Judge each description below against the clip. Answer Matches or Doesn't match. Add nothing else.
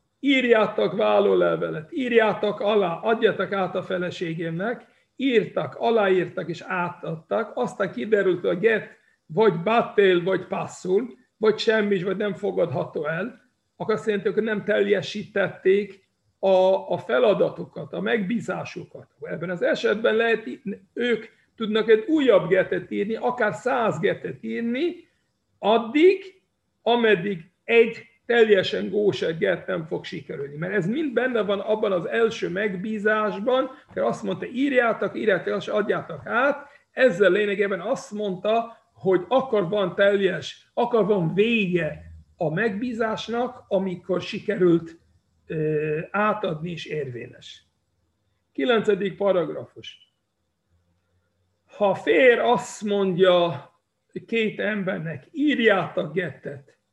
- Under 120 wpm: Matches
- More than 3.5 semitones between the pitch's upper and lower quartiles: Matches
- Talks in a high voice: Matches